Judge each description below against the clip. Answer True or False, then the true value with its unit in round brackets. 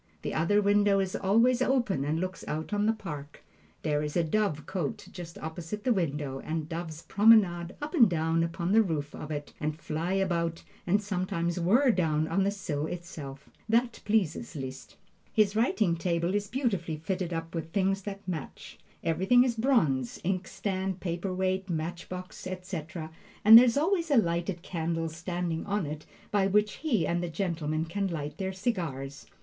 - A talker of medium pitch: True (180 Hz)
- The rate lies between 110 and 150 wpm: False (175 wpm)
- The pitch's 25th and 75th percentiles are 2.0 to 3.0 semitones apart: False (4.0 semitones)